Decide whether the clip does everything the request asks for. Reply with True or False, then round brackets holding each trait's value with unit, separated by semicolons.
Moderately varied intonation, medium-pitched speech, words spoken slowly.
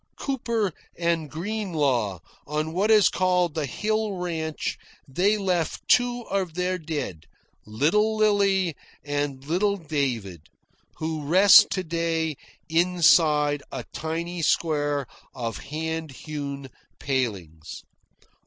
True (4.3 semitones; 160 Hz; 105 wpm)